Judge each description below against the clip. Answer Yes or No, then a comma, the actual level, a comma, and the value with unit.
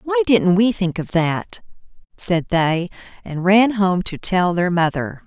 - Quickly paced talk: No, average, 170 wpm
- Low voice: No, high, 190 Hz